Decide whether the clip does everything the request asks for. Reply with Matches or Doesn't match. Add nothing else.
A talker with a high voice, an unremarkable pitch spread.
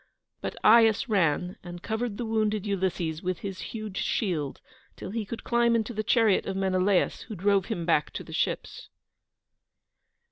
Matches